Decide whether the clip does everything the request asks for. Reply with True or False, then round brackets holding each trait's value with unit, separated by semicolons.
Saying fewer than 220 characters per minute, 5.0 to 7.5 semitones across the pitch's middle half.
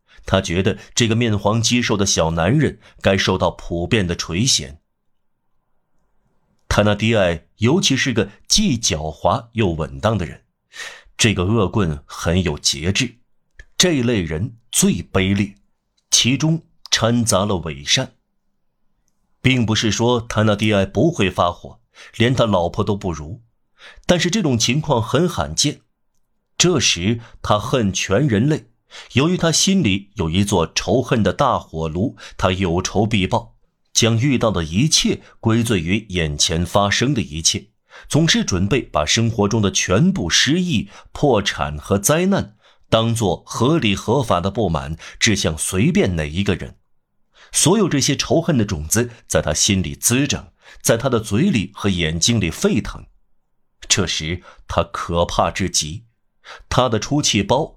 True (210 characters per minute; 5.3 semitones)